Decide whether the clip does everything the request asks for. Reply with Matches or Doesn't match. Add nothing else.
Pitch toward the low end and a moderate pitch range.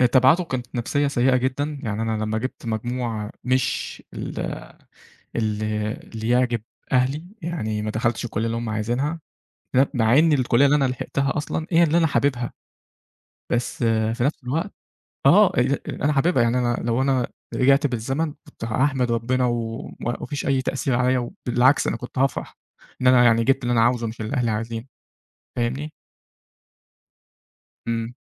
Matches